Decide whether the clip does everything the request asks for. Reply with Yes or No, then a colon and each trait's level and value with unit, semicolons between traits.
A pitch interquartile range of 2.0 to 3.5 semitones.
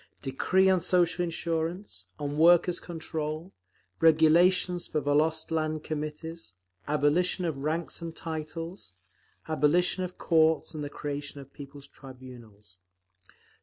Yes: average, 2.7 semitones